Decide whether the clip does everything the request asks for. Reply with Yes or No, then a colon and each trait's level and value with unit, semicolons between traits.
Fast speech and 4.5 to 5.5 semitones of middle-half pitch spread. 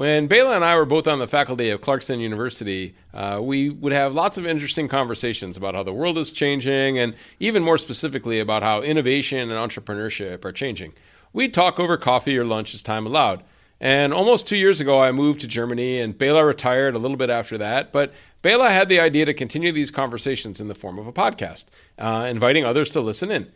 Yes: fast, 215 wpm; average, 4.9 semitones